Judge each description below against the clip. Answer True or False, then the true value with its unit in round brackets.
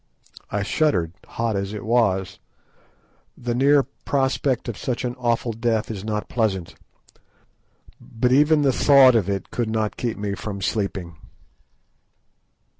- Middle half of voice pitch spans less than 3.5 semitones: False (3.9 semitones)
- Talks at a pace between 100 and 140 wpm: True (135 wpm)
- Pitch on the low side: True (115 Hz)